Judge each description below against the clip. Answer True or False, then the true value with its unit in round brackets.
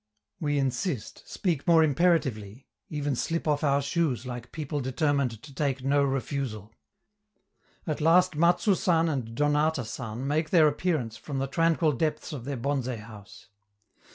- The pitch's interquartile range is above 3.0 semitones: True (3.9 semitones)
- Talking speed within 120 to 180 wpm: True (150 wpm)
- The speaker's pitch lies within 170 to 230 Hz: False (145 Hz)